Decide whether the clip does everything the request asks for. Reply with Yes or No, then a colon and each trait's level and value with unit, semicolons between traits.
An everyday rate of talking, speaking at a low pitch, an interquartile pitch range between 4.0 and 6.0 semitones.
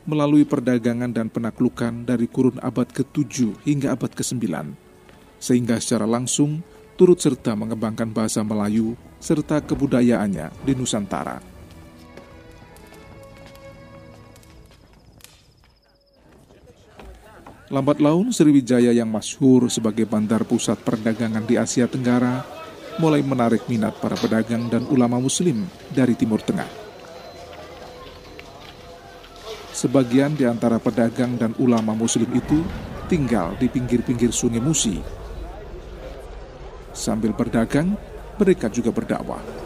No: average, 95 wpm; low, 120 Hz; average, 3.4 semitones